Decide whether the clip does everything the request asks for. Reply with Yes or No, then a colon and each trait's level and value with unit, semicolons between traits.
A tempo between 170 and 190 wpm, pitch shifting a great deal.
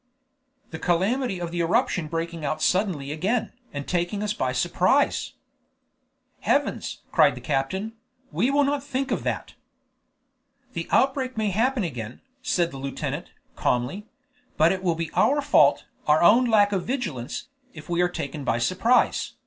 No: average, 155 wpm; wide, 6.6 semitones